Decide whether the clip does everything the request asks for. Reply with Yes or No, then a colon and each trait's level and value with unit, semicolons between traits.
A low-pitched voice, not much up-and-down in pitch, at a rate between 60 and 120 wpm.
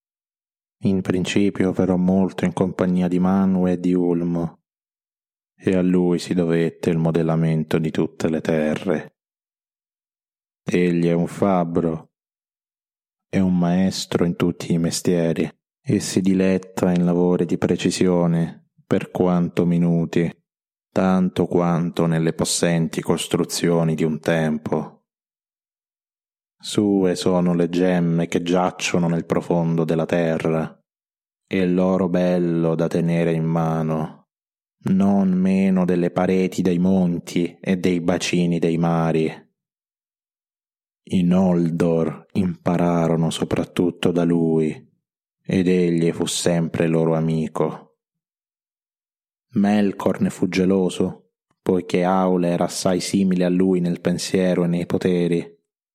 Yes: very low, 90 Hz; narrow, 1.7 semitones; slow, 115 wpm